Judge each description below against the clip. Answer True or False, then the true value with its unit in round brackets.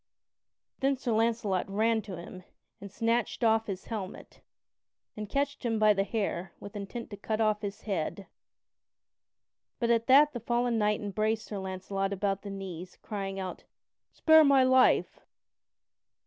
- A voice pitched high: True (215 Hz)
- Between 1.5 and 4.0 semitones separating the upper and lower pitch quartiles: True (3.1 semitones)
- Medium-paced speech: True (150 wpm)